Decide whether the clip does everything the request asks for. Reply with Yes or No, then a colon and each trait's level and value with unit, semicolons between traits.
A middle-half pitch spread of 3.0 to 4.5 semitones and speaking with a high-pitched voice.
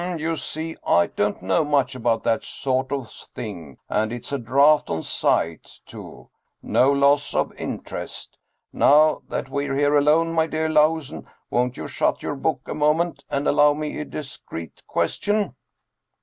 No: average, 4.0 semitones; medium, 140 Hz